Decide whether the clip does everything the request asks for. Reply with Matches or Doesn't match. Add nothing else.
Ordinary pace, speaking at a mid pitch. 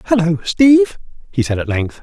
Matches